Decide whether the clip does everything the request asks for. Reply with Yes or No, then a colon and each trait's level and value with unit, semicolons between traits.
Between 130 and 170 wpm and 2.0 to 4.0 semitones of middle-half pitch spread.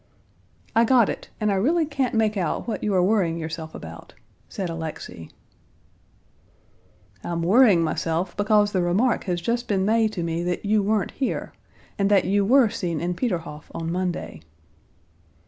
No: average, 165 wpm; average, 4.5 semitones